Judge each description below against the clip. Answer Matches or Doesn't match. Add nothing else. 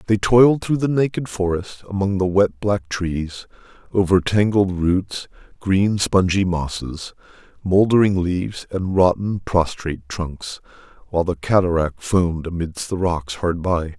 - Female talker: Doesn't match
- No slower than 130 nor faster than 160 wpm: Matches